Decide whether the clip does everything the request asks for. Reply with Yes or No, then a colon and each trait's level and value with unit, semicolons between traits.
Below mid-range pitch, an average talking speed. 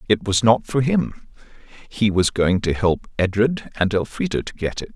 Yes: low, 110 Hz; average, 195 wpm